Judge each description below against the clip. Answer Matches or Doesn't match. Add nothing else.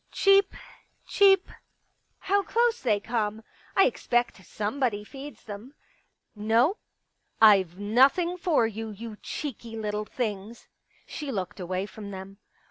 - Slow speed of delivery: Matches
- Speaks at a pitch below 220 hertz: Doesn't match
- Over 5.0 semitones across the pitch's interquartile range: Matches